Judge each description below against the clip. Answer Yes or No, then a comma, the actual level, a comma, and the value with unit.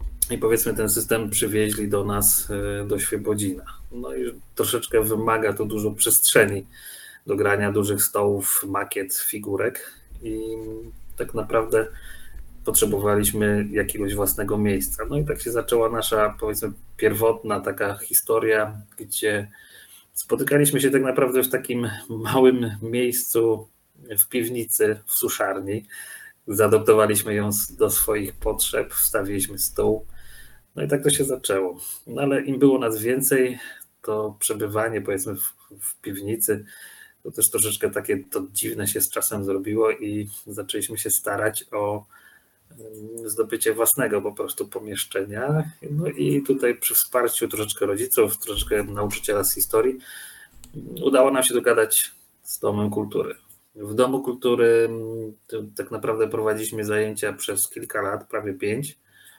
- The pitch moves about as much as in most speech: Yes, average, 3.7 semitones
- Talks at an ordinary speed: Yes, average, 130 wpm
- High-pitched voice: No, low, 110 Hz